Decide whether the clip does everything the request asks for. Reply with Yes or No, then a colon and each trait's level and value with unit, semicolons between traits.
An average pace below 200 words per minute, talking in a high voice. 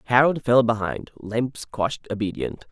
No: slow, 135 wpm; low, 115 Hz